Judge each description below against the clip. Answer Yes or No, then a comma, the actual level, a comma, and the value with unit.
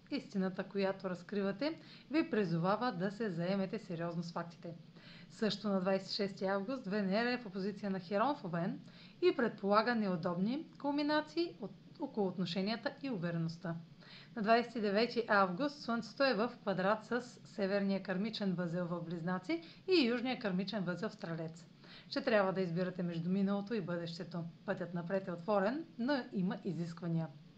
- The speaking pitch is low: No, high, 195 Hz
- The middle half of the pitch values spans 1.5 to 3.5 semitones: No, average, 4.2 semitones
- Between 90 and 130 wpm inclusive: No, average, 145 wpm